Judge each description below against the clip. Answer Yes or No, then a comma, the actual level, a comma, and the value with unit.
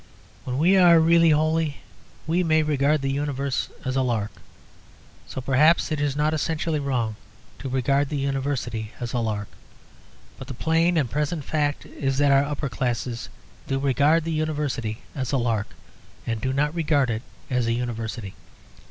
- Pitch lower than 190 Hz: Yes, medium, 140 Hz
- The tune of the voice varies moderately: Yes, average, 3.7 semitones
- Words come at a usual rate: Yes, average, 170 wpm